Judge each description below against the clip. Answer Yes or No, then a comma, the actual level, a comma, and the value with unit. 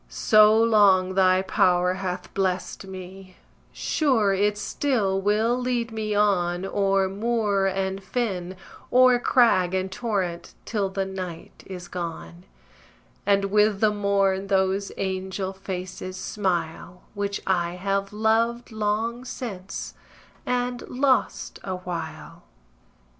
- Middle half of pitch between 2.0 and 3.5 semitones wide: Yes, narrow, 2.5 semitones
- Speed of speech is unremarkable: No, slow, 115 wpm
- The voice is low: No, high, 195 Hz